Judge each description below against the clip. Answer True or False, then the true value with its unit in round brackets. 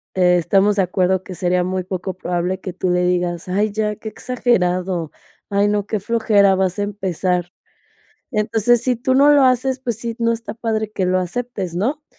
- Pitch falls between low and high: False (200 Hz)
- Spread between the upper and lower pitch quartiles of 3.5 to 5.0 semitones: True (3.9 semitones)